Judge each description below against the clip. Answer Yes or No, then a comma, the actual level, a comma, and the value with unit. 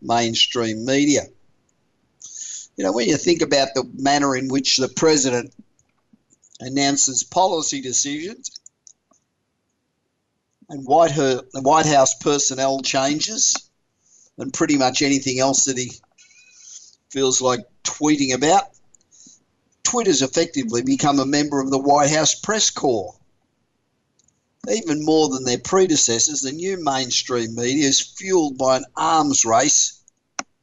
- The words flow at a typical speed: No, slow, 120 wpm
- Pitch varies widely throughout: No, average, 3.0 semitones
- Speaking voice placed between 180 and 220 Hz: No, medium, 140 Hz